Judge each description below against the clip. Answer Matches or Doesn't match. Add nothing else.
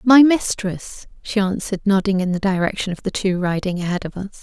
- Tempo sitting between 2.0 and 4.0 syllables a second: Doesn't match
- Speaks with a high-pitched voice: Matches